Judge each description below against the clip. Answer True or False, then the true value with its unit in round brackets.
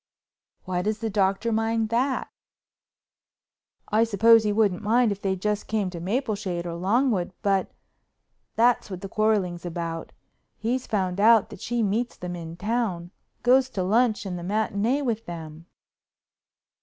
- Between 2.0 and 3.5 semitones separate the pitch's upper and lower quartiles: False (3.9 semitones)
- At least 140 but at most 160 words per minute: True (145 wpm)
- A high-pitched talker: True (210 Hz)